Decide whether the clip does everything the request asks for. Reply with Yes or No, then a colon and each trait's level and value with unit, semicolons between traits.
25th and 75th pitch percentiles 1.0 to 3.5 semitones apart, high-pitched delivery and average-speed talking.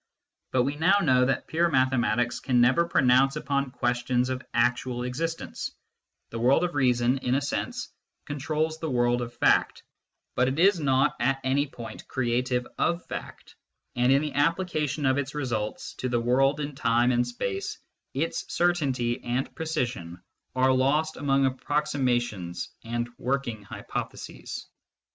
No: average, 3.1 semitones; low, 130 Hz; average, 150 wpm